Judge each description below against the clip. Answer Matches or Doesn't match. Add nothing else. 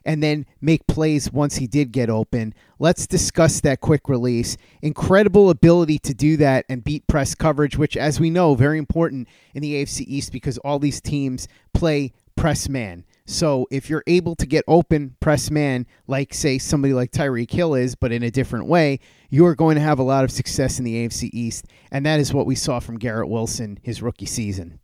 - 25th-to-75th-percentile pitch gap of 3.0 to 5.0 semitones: Matches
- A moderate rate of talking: Doesn't match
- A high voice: Doesn't match